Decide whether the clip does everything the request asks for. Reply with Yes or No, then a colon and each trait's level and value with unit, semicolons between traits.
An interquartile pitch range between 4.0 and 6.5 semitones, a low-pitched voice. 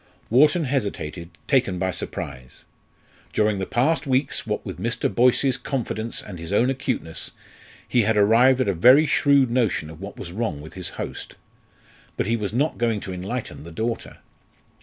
Yes: wide, 5.6 semitones; low, 115 Hz